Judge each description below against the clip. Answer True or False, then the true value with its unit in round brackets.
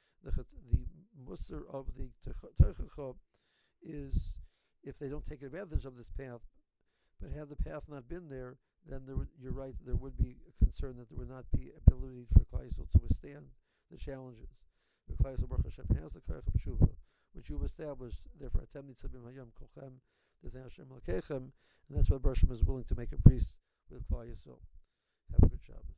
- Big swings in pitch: True (7.3 semitones)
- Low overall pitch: True (130 Hz)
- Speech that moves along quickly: False (160 wpm)